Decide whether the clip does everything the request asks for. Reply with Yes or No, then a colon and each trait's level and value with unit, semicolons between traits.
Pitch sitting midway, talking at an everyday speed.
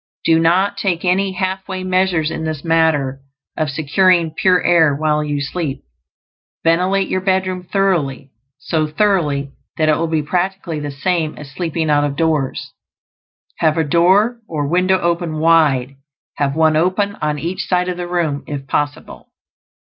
Yes: medium, 165 Hz; average, 160 wpm